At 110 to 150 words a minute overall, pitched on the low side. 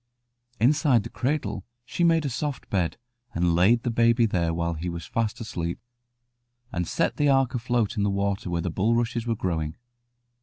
No: average, 180 wpm; low, 110 Hz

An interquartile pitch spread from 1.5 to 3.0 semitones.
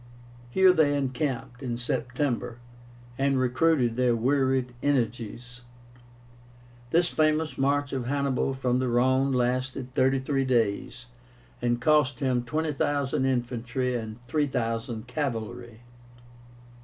Yes: narrow, 2.5 semitones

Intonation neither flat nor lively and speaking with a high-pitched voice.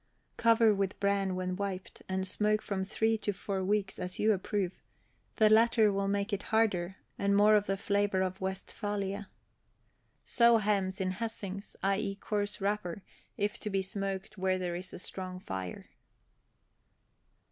No: narrow, 1.8 semitones; high, 200 Hz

